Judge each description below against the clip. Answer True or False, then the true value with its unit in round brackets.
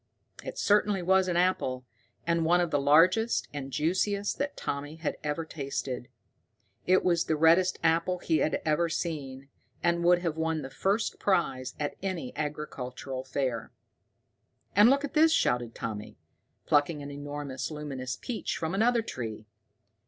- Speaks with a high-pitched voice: False (160 Hz)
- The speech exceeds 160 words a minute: False (150 wpm)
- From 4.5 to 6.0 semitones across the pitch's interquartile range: True (4.8 semitones)